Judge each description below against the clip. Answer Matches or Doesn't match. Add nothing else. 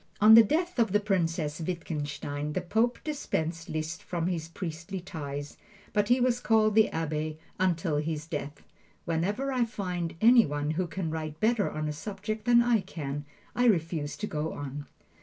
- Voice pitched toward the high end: Doesn't match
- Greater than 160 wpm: Matches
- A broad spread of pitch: Matches